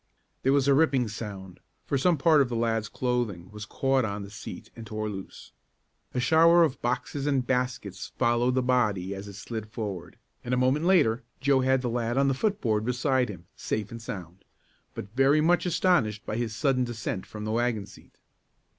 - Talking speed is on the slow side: No, average, 200 wpm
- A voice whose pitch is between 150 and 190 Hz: No, low, 120 Hz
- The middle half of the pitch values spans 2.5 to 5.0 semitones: Yes, average, 3.9 semitones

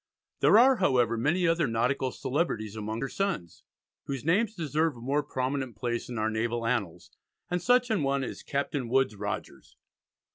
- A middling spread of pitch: No, wide, 6.0 semitones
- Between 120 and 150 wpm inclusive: No, average, 170 wpm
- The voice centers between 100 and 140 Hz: Yes, low, 135 Hz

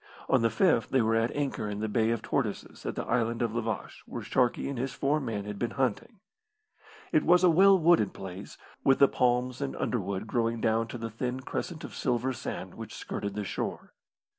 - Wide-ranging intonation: No, average, 3.3 semitones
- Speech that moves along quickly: Yes, fast, 215 wpm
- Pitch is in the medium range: No, low, 120 Hz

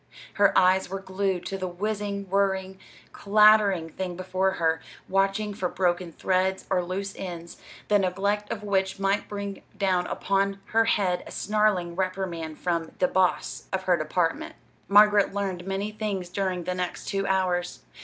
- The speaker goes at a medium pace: Yes, average, 155 wpm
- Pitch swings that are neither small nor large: No, narrow, 1.8 semitones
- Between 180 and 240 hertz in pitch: Yes, high, 190 Hz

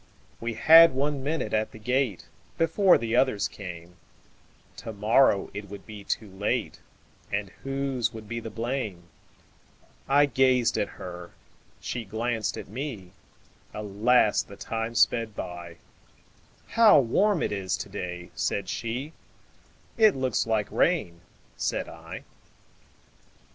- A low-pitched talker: Yes, low, 115 Hz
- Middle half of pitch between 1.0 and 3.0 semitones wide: No, average, 4.7 semitones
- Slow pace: Yes, slow, 110 wpm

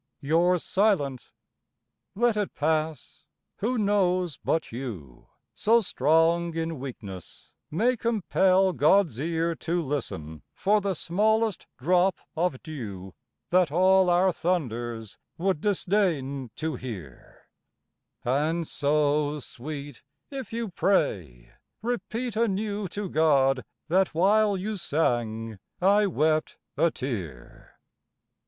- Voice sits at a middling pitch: Yes, medium, 165 Hz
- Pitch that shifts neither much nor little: No, wide, 6.2 semitones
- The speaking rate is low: Yes, slow, 105 wpm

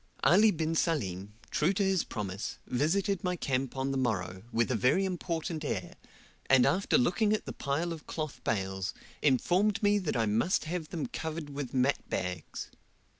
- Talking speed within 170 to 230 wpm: Yes, average, 175 wpm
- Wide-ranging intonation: Yes, wide, 7.0 semitones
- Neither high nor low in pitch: Yes, medium, 150 Hz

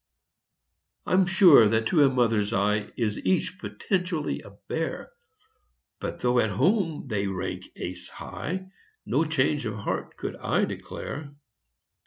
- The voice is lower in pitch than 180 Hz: Yes, low, 135 Hz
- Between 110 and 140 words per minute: Yes, slow, 135 wpm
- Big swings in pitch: Yes, wide, 8.6 semitones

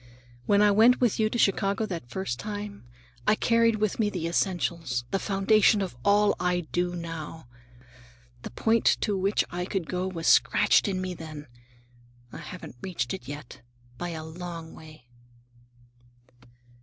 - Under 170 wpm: Yes, average, 155 wpm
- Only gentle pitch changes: No, average, 4.0 semitones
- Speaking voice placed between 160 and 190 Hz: Yes, medium, 185 Hz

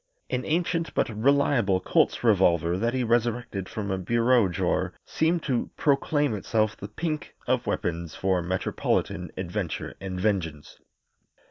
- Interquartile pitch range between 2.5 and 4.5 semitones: No, wide, 5.5 semitones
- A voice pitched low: Yes, low, 110 Hz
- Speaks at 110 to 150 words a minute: Yes, slow, 135 wpm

